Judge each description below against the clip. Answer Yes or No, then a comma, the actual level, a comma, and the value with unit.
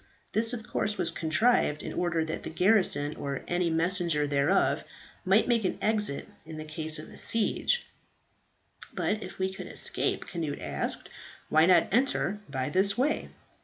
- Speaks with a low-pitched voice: No, medium, 180 Hz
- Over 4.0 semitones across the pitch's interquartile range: Yes, average, 5.2 semitones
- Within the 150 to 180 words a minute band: Yes, average, 155 wpm